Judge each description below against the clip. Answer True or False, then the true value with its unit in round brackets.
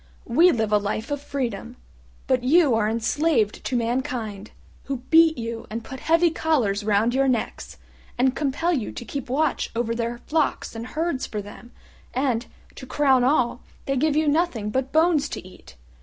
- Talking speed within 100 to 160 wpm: False (175 wpm)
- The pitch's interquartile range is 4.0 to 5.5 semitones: True (4.4 semitones)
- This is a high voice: True (255 Hz)